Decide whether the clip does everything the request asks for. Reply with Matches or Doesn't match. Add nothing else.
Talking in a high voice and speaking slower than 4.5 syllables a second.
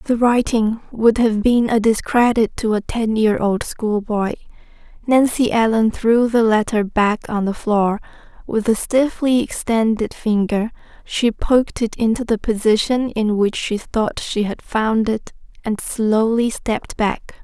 Matches